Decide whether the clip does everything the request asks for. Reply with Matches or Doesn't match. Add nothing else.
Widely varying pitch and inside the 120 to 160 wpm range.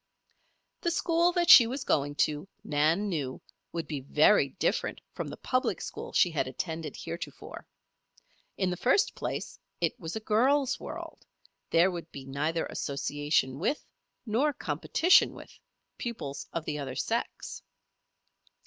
Matches